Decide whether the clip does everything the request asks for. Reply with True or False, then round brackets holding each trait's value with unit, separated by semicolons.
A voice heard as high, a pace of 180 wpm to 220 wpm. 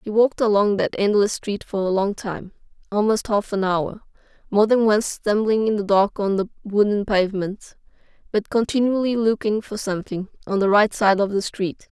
True (205 Hz; 185 wpm)